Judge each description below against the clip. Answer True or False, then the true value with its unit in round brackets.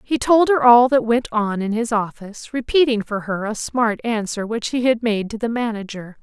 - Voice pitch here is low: False (230 Hz)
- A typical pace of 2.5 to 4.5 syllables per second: False (4.9 syllables/s)